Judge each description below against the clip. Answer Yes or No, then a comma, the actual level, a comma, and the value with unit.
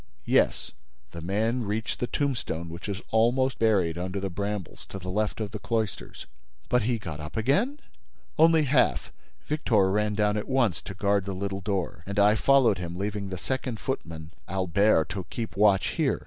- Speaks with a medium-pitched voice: No, low, 105 Hz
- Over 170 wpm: Yes, average, 180 wpm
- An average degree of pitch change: Yes, average, 3.6 semitones